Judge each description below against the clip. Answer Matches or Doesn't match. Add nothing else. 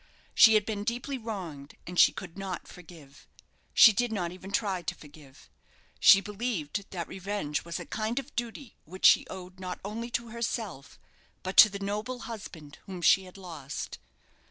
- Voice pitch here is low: Doesn't match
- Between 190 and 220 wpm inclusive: Doesn't match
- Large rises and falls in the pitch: Doesn't match